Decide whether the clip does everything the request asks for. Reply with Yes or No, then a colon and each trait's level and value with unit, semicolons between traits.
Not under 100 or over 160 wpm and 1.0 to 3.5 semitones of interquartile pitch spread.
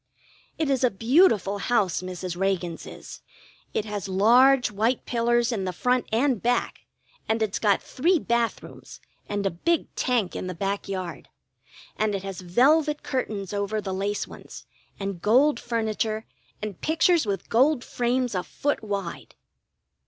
No: average, 155 wpm; average, 4.2 semitones